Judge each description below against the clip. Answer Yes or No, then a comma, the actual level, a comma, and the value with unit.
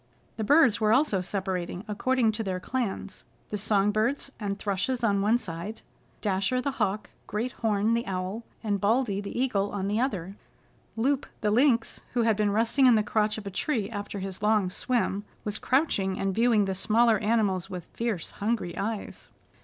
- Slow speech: No, average, 185 wpm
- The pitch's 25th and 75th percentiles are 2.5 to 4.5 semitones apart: Yes, average, 2.9 semitones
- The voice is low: No, high, 210 Hz